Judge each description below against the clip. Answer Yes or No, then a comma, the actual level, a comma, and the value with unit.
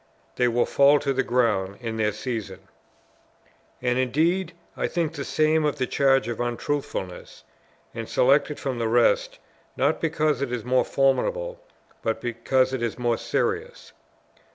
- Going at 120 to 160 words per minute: Yes, average, 155 wpm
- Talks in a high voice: No, low, 130 Hz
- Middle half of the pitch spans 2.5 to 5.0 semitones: Yes, average, 4.1 semitones